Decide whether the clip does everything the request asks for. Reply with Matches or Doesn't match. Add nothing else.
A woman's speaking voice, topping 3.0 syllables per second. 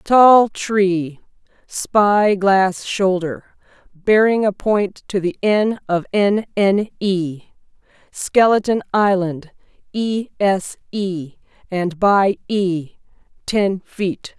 Doesn't match